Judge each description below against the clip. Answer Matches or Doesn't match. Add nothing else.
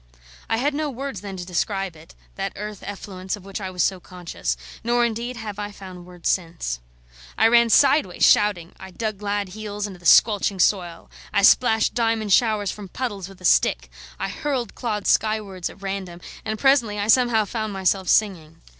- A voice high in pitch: Matches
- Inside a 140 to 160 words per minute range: Doesn't match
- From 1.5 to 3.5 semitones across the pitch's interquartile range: Matches